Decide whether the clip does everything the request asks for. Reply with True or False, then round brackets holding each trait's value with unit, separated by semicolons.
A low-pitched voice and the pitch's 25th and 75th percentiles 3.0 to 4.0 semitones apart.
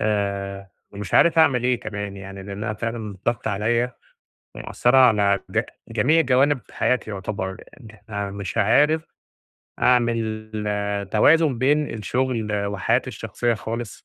True (110 Hz; 3.5 semitones)